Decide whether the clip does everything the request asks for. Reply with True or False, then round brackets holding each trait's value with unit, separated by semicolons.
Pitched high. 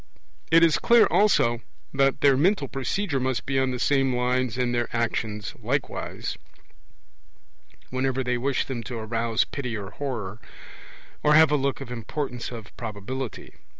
False (130 Hz)